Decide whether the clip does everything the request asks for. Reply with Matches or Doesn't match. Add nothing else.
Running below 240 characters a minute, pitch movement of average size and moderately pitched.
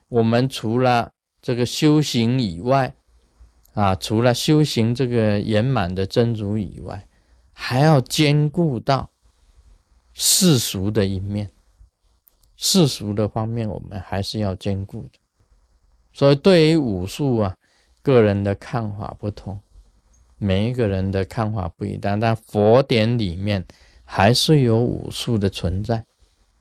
Doesn't match